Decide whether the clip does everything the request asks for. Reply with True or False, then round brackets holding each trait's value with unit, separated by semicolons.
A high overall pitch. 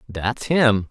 False (115 Hz)